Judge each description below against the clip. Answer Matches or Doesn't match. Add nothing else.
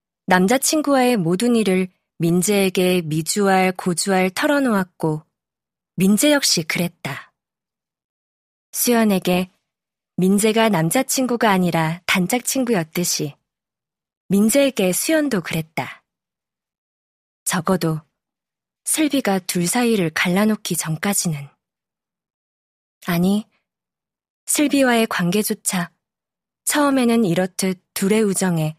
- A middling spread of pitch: Matches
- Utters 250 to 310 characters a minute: Doesn't match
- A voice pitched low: Doesn't match